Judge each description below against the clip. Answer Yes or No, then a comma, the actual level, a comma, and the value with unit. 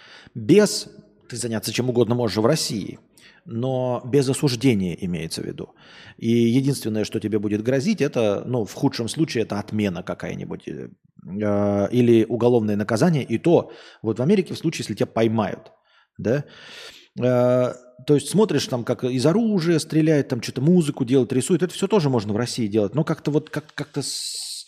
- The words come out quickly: Yes, fast, 165 wpm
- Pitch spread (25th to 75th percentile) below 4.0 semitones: No, average, 4.5 semitones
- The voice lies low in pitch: Yes, low, 125 Hz